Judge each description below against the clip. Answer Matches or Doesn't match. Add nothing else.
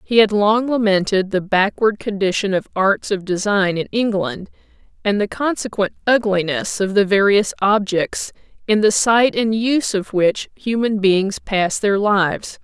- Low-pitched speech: Doesn't match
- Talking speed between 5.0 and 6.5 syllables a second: Doesn't match